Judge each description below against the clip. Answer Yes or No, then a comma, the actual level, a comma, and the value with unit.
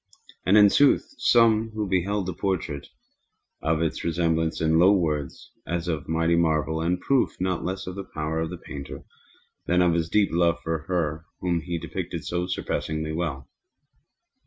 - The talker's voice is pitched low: Yes, very low, 85 Hz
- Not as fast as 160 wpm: No, average, 180 wpm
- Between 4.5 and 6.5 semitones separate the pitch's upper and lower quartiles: No, narrow, 2.5 semitones